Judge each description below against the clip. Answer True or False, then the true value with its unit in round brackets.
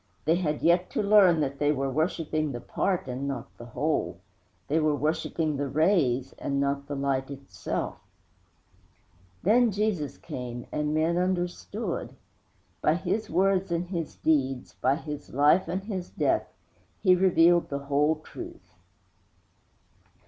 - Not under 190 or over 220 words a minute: False (140 wpm)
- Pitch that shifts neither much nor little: True (4.4 semitones)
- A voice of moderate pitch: True (155 Hz)